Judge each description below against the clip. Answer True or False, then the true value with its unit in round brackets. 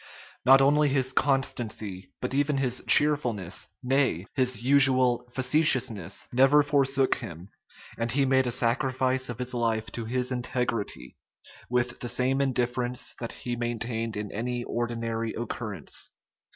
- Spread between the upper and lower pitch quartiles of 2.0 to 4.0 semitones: True (2.4 semitones)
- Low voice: True (125 Hz)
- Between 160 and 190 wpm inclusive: False (135 wpm)